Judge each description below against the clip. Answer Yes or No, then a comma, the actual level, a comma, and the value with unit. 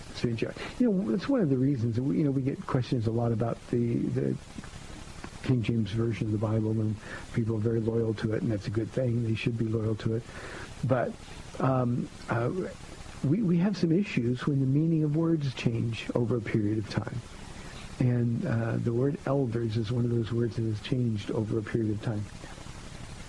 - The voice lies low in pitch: Yes, low, 120 Hz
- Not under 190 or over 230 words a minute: Yes, fast, 205 wpm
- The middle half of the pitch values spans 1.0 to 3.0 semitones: Yes, average, 2.7 semitones